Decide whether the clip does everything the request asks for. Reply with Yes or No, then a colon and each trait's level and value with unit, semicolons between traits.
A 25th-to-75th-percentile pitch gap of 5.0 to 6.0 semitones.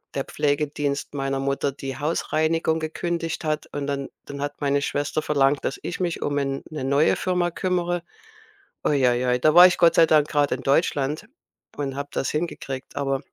No: average, 2.7 semitones